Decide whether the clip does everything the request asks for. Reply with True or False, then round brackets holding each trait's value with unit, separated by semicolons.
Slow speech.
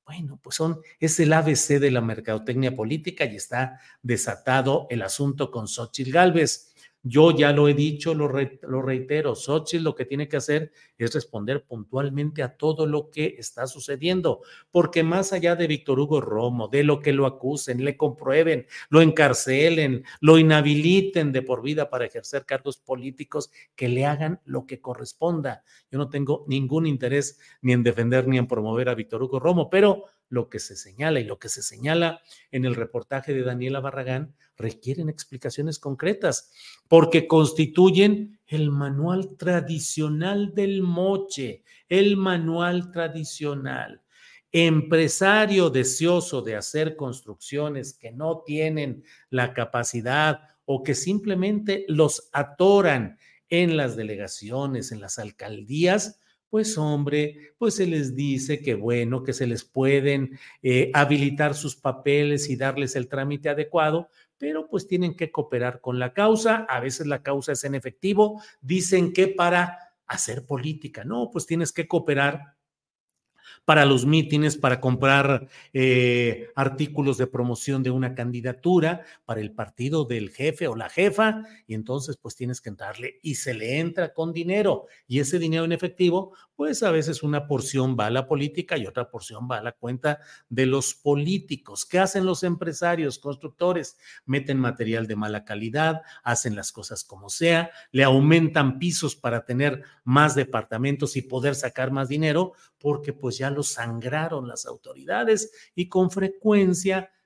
False (155 wpm)